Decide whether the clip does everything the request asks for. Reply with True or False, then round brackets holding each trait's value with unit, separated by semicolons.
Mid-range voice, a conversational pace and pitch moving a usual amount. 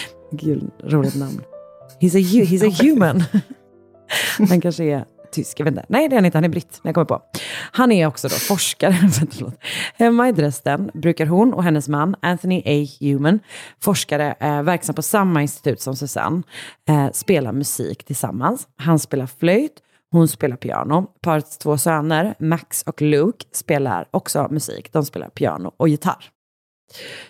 True (160 Hz; 155 wpm; 4.4 semitones)